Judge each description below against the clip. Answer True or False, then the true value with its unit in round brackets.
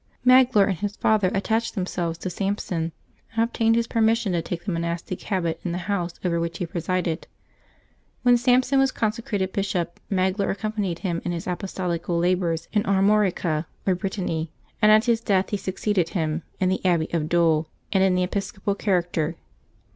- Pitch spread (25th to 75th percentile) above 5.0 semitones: False (3.5 semitones)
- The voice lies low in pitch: False (185 Hz)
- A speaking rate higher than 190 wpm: False (175 wpm)